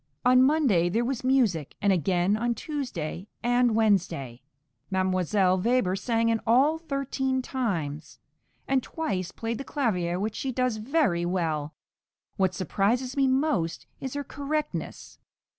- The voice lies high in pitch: Yes, high, 225 Hz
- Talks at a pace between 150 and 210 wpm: No, slow, 135 wpm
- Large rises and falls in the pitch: Yes, wide, 6.2 semitones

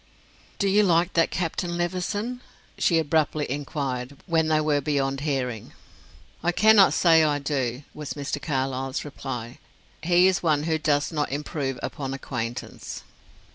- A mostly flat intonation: No, average, 3.9 semitones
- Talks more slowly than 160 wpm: Yes, average, 140 wpm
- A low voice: No, medium, 150 Hz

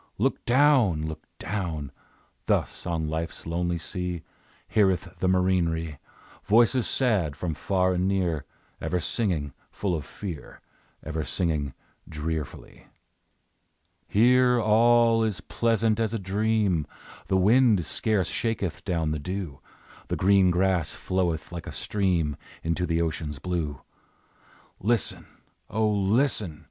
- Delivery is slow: Yes, slow, 120 wpm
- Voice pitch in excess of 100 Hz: No, very low, 90 Hz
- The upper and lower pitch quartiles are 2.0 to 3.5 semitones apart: No, average, 4.7 semitones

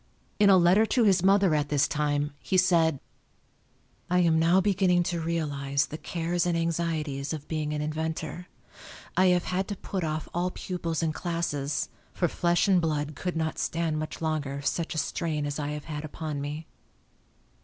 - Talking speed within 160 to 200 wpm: Yes, average, 180 wpm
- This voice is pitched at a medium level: Yes, medium, 160 Hz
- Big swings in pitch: No, average, 2.8 semitones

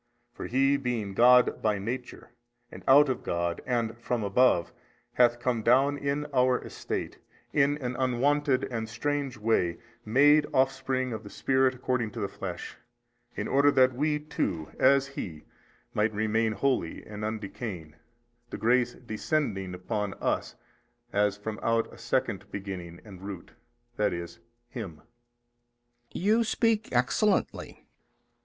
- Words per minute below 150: Yes, average, 140 wpm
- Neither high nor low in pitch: No, low, 120 Hz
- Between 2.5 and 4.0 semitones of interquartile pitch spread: No, average, 4.5 semitones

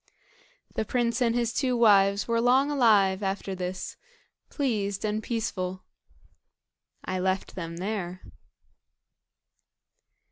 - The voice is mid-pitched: No, high, 210 Hz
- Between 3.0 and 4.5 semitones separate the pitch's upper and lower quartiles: Yes, average, 3.8 semitones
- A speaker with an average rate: No, slow, 105 wpm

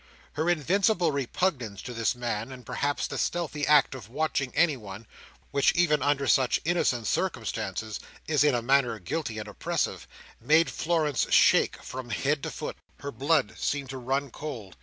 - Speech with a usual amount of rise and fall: Yes, average, 4.1 semitones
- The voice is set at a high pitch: No, medium, 140 Hz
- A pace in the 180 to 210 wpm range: No, average, 160 wpm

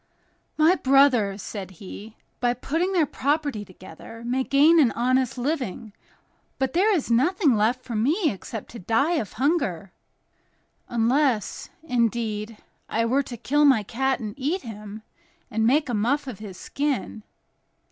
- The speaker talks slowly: No, average, 145 wpm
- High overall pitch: Yes, high, 245 Hz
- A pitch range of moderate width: Yes, average, 4.7 semitones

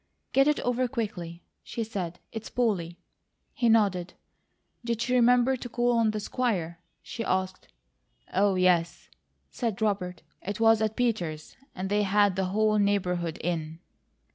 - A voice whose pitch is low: No, high, 205 Hz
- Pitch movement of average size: Yes, average, 4.4 semitones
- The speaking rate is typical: Yes, average, 145 wpm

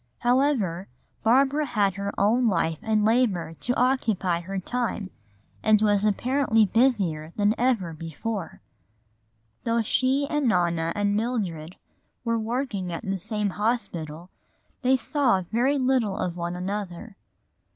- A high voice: Yes, high, 210 Hz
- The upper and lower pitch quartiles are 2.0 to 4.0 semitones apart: No, average, 5.2 semitones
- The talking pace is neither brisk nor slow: No, slow, 130 wpm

